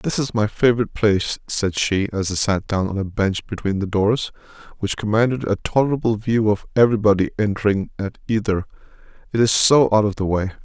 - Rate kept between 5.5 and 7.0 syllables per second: Yes, 5.8 syllables/s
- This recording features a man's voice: Yes, male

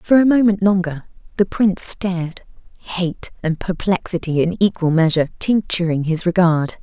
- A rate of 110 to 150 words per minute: Yes, average, 140 wpm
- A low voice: No, medium, 180 Hz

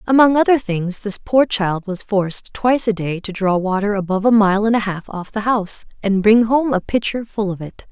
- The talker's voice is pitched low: No, high, 210 Hz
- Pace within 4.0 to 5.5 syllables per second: Yes, 5.3 syllables/s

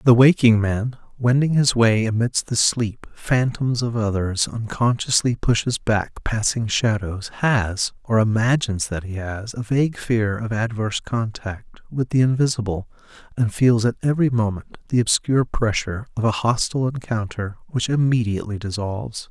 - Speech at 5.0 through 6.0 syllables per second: No, 4.8 syllables/s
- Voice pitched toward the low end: Yes, low, 115 Hz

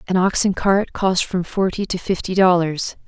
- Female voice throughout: Yes, female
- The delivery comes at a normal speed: Yes, average, 195 wpm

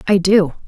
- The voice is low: No, high, 190 Hz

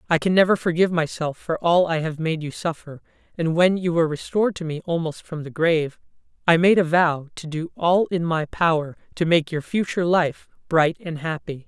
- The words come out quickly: Yes, fast, 210 wpm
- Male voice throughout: No, female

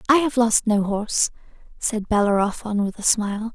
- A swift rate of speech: No, average, 170 wpm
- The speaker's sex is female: Yes, female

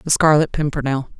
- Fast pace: No, average, 150 wpm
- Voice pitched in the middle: Yes, medium, 145 Hz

